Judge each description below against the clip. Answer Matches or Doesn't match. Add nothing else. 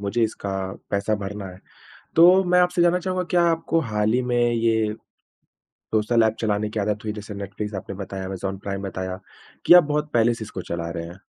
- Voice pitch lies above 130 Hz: Doesn't match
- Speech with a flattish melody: Doesn't match